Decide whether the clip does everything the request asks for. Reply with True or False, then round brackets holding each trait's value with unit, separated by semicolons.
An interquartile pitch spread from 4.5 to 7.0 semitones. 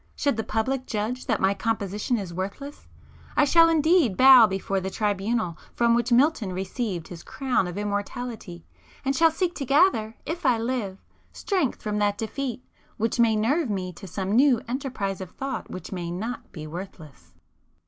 True (5.4 semitones)